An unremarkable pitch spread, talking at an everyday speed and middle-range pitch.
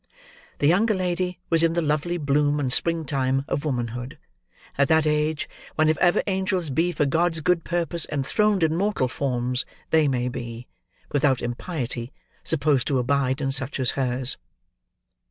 Yes: average, 4.3 semitones; average, 160 wpm; medium, 150 Hz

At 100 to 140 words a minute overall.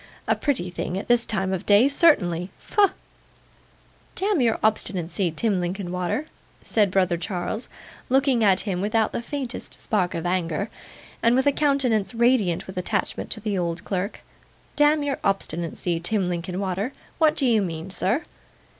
No: average, 155 wpm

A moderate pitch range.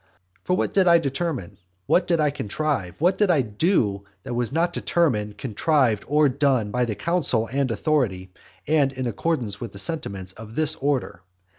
No: wide, 6.8 semitones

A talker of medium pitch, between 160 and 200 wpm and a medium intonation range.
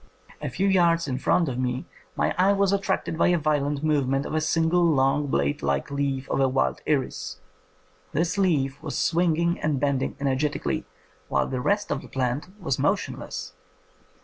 Yes: medium, 150 Hz; average, 175 wpm; average, 4.1 semitones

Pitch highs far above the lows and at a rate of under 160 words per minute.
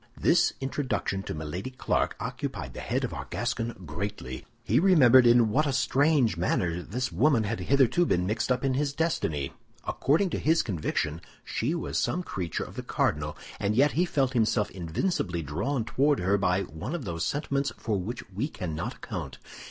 No: wide, 7.7 semitones; average, 180 wpm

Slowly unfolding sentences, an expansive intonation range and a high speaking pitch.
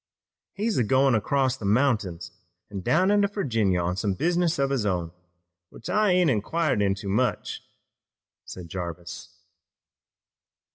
No: slow, 130 wpm; wide, 8.9 semitones; low, 115 Hz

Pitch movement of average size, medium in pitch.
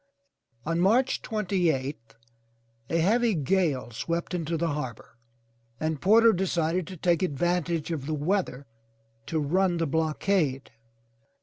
Yes: average, 3.9 semitones; medium, 165 Hz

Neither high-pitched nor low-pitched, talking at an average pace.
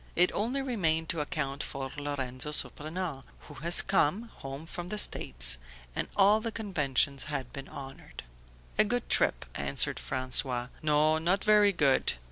Yes: medium, 150 Hz; average, 150 wpm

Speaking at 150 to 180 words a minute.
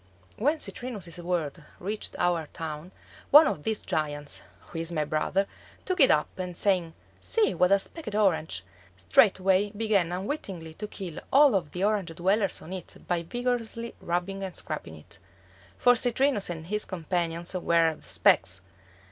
Yes: average, 155 wpm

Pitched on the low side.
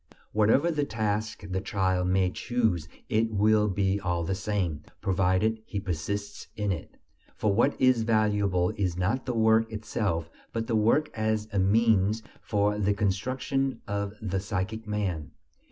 Yes: low, 105 Hz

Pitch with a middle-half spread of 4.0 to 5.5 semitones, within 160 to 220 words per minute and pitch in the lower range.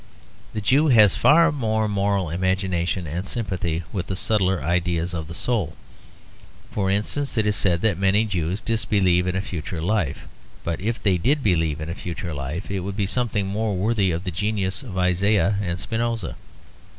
No: average, 3.6 semitones; average, 180 wpm; very low, 95 Hz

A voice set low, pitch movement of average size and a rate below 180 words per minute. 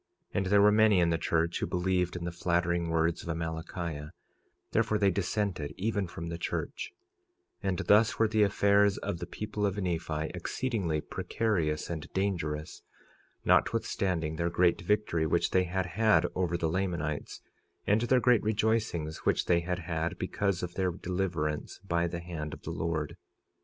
Yes: very low, 90 Hz; average, 3.5 semitones; average, 170 wpm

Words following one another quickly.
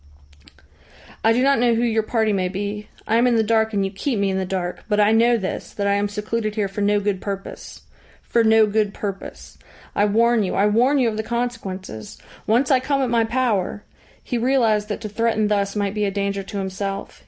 Yes: fast, 230 wpm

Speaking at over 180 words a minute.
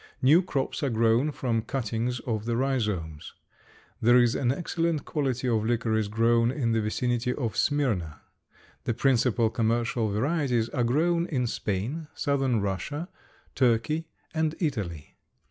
No: slow, 135 wpm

